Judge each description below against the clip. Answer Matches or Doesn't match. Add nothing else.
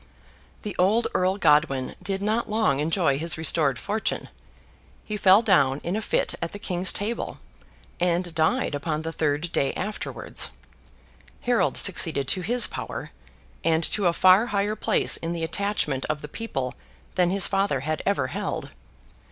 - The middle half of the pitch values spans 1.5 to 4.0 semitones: Doesn't match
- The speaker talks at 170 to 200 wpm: Doesn't match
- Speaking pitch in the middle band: Matches